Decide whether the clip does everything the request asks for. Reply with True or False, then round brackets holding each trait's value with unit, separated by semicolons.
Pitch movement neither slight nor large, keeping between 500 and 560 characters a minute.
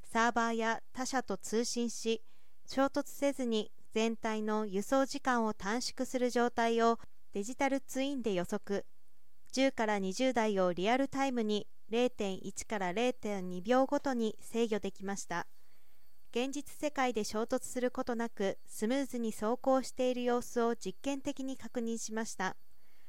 False (3.3 semitones; 265 characters per minute)